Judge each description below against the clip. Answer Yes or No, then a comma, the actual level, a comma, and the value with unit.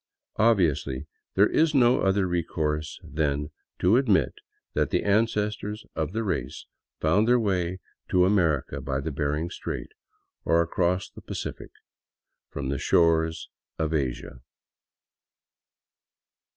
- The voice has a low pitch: Yes, very low, 85 Hz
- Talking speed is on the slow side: Yes, slow, 125 wpm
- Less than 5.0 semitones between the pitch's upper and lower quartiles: No, average, 5.3 semitones